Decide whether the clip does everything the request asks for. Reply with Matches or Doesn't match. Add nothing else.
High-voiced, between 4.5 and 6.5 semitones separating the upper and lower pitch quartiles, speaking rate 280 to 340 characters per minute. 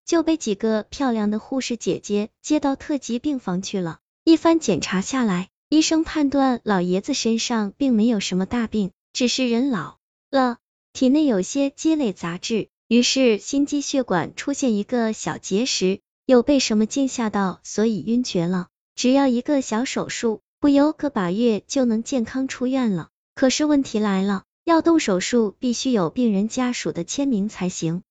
Doesn't match